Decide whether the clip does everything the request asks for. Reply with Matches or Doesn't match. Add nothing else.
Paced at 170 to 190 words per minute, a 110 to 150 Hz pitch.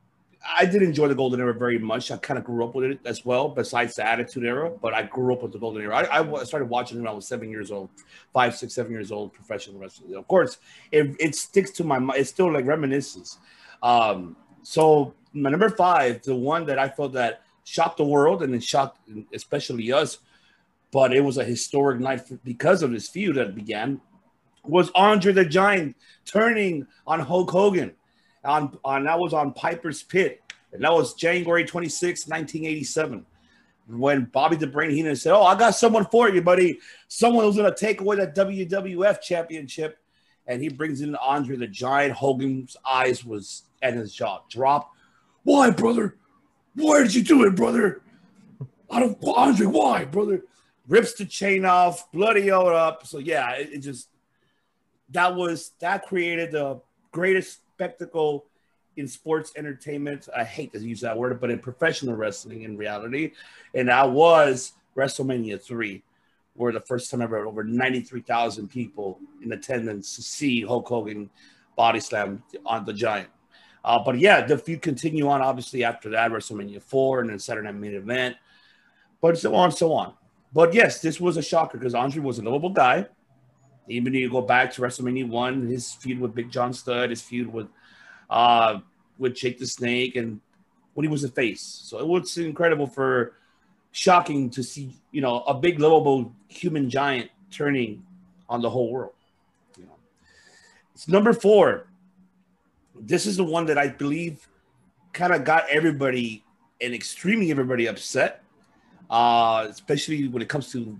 Matches